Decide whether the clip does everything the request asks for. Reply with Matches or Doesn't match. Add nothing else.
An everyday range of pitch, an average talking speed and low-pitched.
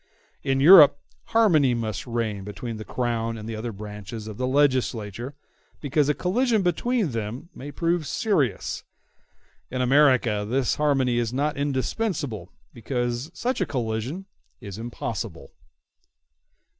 Doesn't match